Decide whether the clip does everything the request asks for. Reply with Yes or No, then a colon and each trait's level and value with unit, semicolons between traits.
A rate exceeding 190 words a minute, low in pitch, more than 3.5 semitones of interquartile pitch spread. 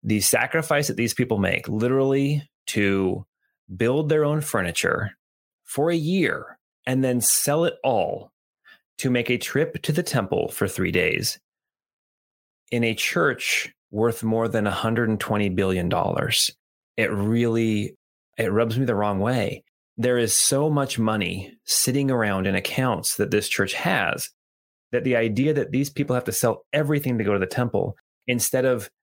No: average, 165 wpm; low, 120 Hz; average, 4.3 semitones